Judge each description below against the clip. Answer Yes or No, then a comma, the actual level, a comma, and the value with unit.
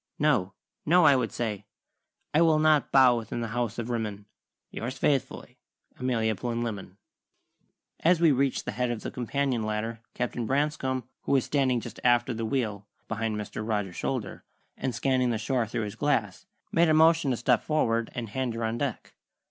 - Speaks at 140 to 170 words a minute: No, average, 180 wpm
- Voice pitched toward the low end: Yes, low, 120 Hz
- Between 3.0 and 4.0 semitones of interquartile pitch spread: Yes, average, 3.5 semitones